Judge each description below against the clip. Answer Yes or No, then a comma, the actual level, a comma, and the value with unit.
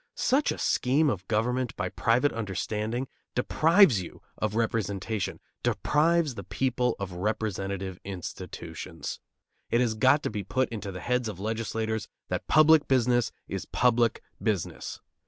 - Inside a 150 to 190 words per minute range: No, average, 140 wpm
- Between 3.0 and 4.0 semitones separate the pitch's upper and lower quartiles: Yes, average, 3.7 semitones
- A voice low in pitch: Yes, low, 115 Hz